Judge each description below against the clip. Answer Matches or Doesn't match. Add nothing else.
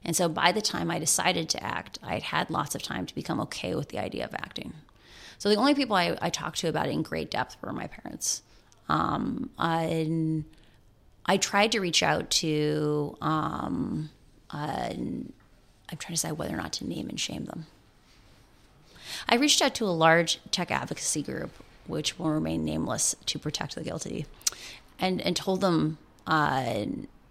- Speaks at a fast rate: Doesn't match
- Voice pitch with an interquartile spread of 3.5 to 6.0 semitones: Matches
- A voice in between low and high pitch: Matches